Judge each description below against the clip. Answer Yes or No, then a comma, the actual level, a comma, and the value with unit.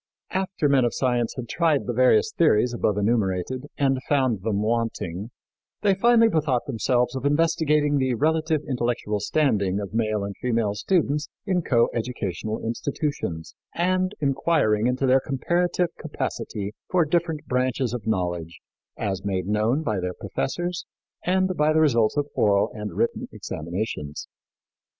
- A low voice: Yes, low, 125 Hz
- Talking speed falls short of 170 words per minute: Yes, average, 140 wpm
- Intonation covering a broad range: Yes, wide, 6.5 semitones